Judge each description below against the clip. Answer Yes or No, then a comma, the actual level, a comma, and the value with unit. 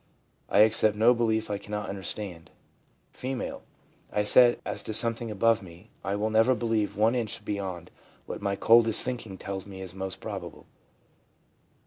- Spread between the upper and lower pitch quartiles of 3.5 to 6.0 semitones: No, narrow, 2.6 semitones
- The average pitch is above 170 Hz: No, low, 105 Hz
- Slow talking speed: No, average, 165 wpm